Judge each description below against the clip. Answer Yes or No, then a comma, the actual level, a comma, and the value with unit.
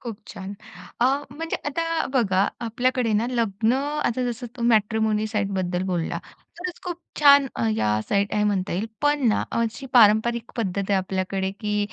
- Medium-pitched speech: No, high, 220 Hz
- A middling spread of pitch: Yes, average, 4.5 semitones